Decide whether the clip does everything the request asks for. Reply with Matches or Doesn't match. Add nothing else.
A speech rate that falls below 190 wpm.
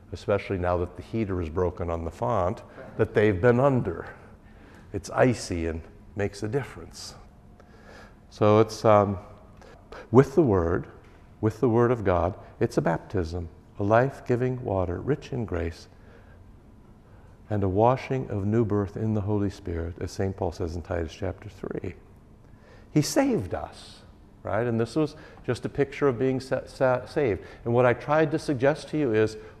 Matches